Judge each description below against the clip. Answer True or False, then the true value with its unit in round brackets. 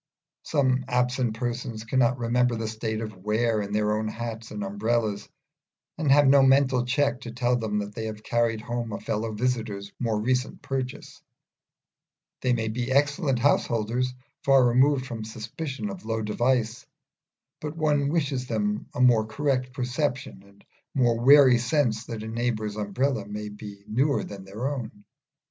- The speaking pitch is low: True (120 Hz)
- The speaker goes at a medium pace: True (165 wpm)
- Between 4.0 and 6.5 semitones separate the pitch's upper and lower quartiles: False (3.2 semitones)